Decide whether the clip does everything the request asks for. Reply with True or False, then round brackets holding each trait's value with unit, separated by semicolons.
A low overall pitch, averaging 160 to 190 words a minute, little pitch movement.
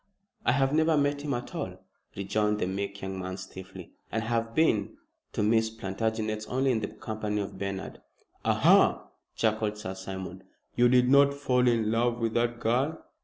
False (110 Hz; 175 wpm; 3.7 semitones)